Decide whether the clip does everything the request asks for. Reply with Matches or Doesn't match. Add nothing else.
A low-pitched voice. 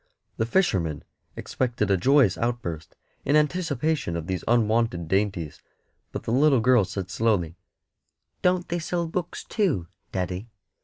Matches